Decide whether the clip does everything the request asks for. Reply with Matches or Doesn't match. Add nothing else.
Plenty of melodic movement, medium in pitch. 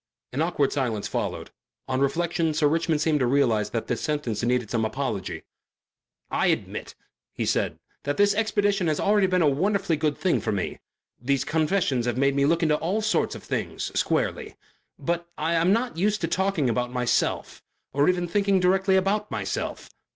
Matches